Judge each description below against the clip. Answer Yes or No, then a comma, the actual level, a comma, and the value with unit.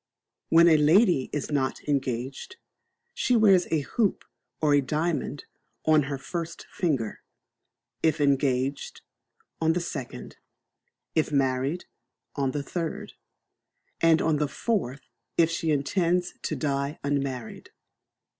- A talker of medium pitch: Yes, medium, 150 Hz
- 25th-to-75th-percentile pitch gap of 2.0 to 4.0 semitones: Yes, average, 3.4 semitones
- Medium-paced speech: No, slow, 115 wpm